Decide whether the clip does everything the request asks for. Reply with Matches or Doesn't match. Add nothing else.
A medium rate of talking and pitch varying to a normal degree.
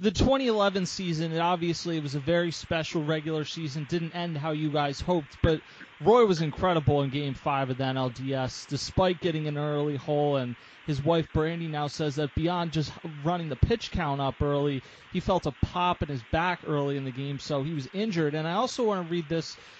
Doesn't match